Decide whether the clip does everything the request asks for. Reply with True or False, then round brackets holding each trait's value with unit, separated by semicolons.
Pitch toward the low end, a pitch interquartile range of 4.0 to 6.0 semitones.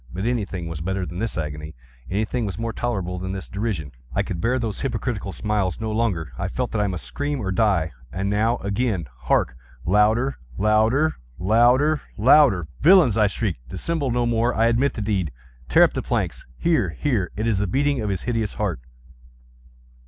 True (105 Hz; 4.6 semitones)